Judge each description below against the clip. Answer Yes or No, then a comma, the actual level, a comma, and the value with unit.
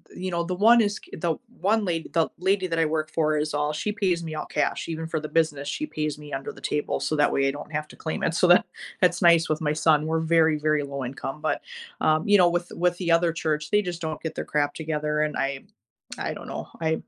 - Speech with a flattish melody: Yes, narrow, 2.3 semitones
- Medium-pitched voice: Yes, medium, 160 Hz